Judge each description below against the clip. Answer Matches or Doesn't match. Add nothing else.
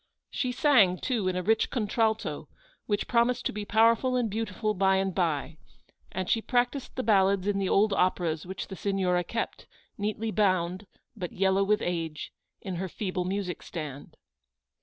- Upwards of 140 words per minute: Matches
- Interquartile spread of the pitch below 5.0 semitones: Matches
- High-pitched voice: Matches